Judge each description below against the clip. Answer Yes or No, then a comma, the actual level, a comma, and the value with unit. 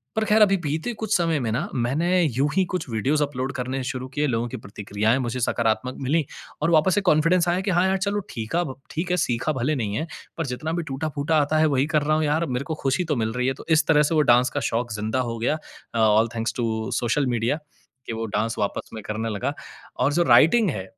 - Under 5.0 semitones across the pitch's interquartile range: No, wide, 5.4 semitones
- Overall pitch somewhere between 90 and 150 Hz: Yes, medium, 140 Hz